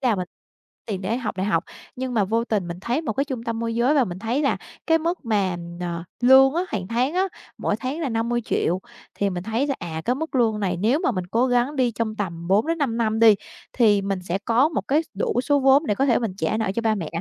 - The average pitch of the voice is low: No, high, 230 Hz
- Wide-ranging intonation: No, average, 4.8 semitones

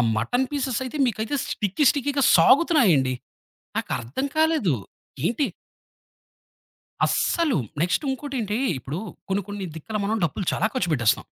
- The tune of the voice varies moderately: No, wide, 8.2 semitones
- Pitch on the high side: Yes, high, 220 Hz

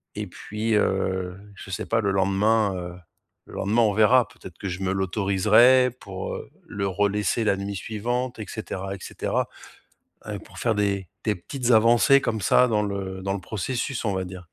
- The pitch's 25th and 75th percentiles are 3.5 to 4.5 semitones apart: No, average, 2.8 semitones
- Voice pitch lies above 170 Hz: No, low, 100 Hz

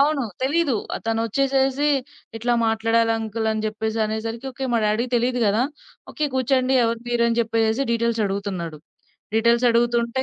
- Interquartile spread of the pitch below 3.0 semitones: Yes, narrow, 2.5 semitones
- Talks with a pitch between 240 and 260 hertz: No, high, 230 Hz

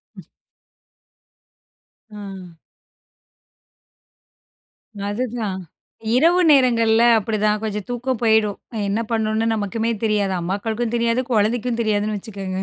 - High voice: Yes, high, 220 Hz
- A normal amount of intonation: No, narrow, 2.2 semitones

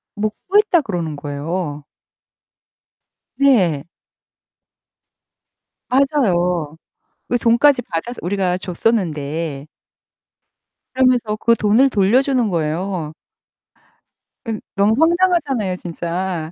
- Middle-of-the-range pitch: No, high, 195 Hz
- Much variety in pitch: Yes, wide, 6.9 semitones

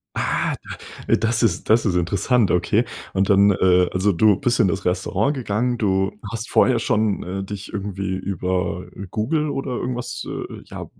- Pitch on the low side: Yes, low, 100 Hz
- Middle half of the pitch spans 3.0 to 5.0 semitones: Yes, average, 3.8 semitones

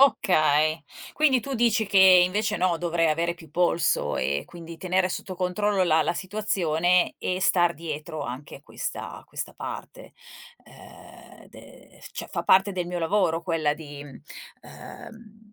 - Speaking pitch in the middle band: Yes, medium, 175 Hz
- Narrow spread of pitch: No, average, 3.6 semitones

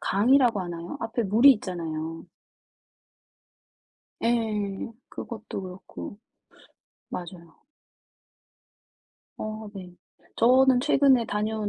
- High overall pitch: Yes, high, 215 Hz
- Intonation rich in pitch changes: No, average, 4.5 semitones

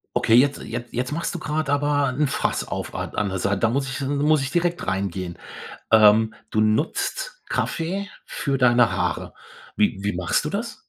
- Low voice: Yes, low, 125 Hz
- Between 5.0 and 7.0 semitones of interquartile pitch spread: Yes, wide, 5.4 semitones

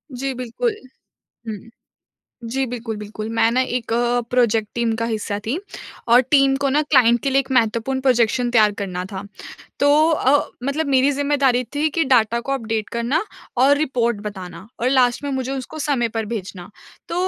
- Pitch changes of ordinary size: Yes, average, 3.4 semitones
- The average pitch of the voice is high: Yes, high, 245 Hz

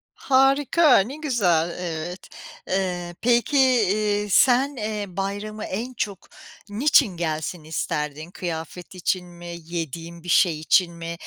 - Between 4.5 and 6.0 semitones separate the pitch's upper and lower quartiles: Yes, average, 5.2 semitones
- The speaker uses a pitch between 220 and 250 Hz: No, medium, 185 Hz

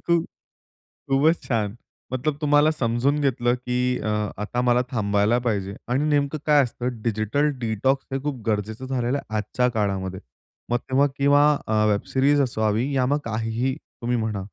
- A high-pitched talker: No, low, 125 Hz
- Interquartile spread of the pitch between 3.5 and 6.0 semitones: Yes, average, 4.1 semitones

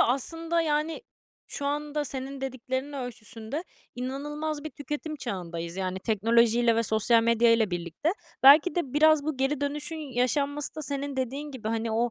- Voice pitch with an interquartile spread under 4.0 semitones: No, average, 4.3 semitones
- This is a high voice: Yes, very high, 270 Hz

